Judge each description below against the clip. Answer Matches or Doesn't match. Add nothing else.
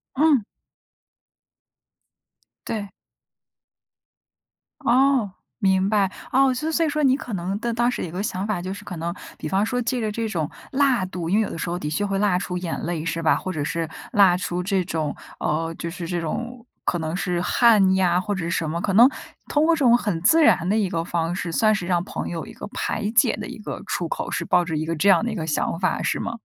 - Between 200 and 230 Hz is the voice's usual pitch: Doesn't match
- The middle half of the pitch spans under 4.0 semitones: Doesn't match